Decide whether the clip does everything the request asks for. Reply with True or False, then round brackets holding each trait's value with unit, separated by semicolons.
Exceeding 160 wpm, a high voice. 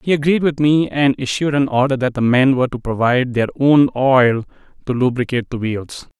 False (205 wpm; 130 Hz)